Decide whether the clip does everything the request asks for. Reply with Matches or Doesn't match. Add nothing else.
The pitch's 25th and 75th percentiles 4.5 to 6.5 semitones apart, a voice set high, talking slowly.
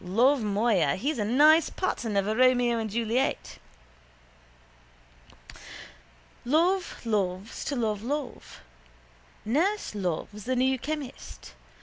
Matches